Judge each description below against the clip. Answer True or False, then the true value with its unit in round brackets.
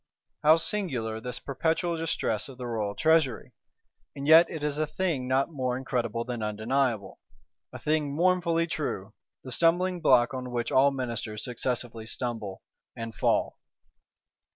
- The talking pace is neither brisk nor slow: True (145 wpm)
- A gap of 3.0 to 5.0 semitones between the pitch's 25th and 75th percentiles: False (5.4 semitones)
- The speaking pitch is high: False (130 Hz)